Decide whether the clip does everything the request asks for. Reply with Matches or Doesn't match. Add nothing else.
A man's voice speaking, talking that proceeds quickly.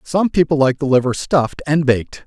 Matches